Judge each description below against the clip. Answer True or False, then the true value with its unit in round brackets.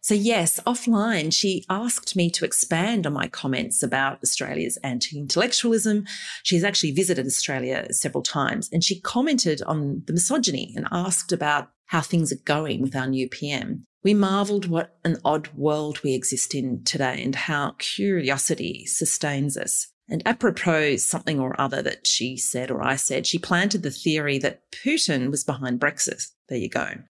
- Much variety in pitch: True (6.0 semitones)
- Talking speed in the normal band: True (170 wpm)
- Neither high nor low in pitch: True (160 Hz)